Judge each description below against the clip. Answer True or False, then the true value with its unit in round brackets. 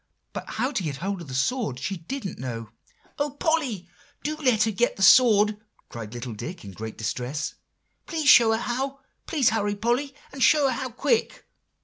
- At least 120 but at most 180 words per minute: False (190 wpm)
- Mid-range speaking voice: False (220 Hz)